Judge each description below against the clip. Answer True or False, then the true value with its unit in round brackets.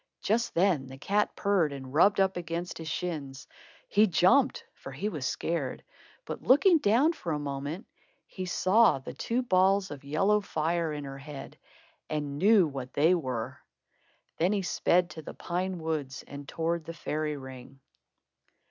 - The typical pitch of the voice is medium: True (165 Hz)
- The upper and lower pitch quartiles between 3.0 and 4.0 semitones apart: False (5.4 semitones)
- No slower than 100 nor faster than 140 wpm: False (165 wpm)